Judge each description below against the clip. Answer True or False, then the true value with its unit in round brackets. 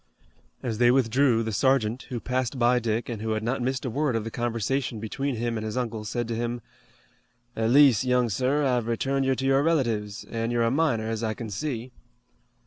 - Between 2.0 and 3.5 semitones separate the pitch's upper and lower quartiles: True (2.7 semitones)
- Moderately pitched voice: False (120 Hz)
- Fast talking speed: True (215 wpm)